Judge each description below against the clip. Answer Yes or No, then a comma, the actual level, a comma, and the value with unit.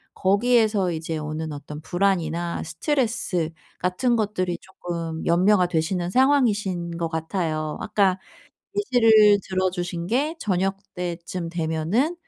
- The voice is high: No, medium, 180 Hz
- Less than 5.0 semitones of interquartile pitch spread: Yes, average, 4.0 semitones